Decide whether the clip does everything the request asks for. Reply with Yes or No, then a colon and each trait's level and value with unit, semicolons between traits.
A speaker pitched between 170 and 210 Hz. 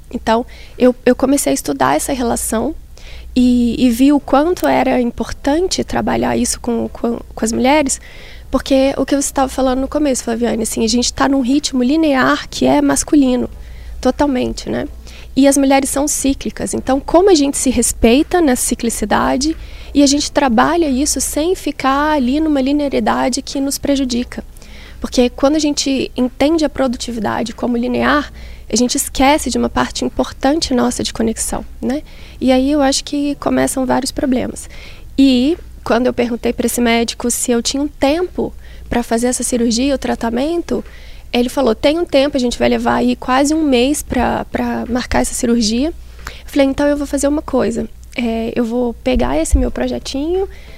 No: very high, 265 Hz